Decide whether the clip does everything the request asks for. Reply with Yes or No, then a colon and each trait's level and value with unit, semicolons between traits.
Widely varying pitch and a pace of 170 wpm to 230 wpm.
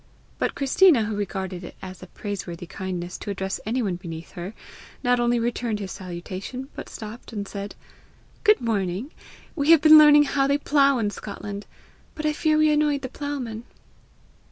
Yes: wide, 6.7 semitones; average, 175 wpm